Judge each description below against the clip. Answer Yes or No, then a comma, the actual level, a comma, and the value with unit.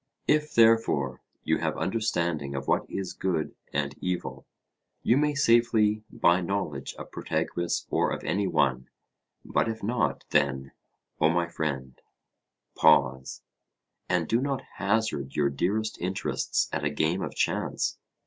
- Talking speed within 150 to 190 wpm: No, average, 140 wpm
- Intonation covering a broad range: Yes, wide, 7.4 semitones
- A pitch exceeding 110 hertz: No, very low, 90 Hz